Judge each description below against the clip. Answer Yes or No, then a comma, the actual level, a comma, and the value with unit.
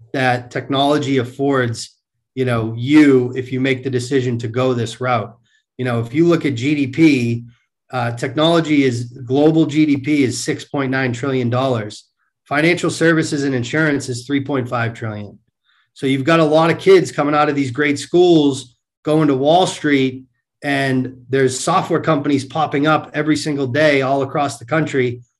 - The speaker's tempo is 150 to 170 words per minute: Yes, average, 160 wpm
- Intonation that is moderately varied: Yes, average, 3.1 semitones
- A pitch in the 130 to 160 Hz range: Yes, low, 135 Hz